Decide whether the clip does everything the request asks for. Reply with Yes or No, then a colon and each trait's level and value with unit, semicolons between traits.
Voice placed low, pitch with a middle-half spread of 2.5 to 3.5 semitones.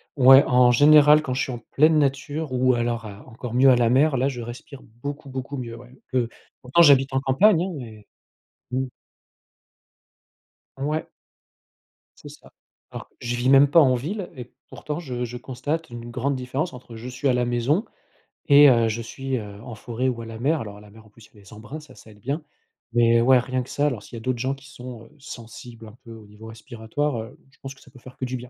Yes: low, 125 Hz; average, 2.9 semitones